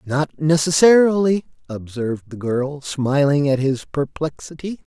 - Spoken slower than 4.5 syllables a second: Yes, 4.3 syllables/s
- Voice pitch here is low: No, medium, 145 Hz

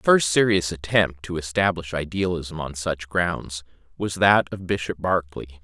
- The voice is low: Yes, very low, 85 Hz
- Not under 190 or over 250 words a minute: No, average, 160 wpm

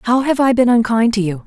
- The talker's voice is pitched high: Yes, high, 235 Hz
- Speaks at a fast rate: Yes, fast, 285 wpm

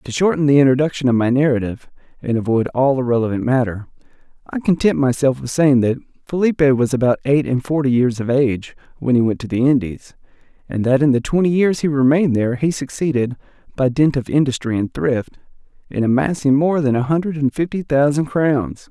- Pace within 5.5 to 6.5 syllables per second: Yes, 5.9 syllables/s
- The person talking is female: No, male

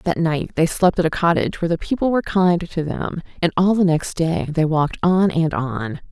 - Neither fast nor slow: No, fast, 235 wpm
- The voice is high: No, medium, 170 Hz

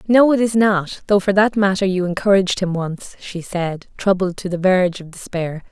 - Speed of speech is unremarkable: No, fast, 210 wpm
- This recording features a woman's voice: Yes, female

